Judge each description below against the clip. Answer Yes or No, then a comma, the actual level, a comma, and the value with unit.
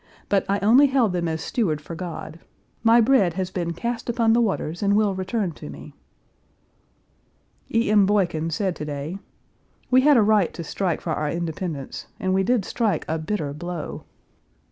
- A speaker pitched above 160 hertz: Yes, high, 190 Hz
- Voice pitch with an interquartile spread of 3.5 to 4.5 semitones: No, average, 5.1 semitones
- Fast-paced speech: No, average, 180 wpm